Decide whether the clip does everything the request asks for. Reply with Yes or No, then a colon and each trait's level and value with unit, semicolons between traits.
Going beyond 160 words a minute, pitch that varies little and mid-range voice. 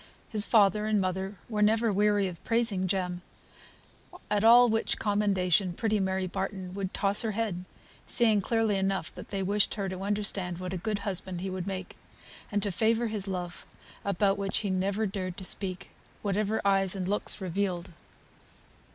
No: average, 170 wpm; narrow, 2.0 semitones; high, 195 Hz